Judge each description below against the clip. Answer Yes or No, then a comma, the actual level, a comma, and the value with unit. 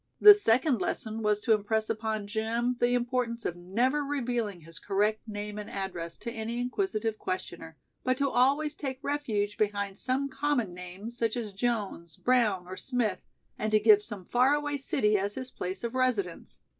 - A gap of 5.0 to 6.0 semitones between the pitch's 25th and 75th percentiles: No, average, 3.7 semitones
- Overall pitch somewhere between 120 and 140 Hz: No, high, 220 Hz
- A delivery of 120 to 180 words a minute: Yes, average, 170 wpm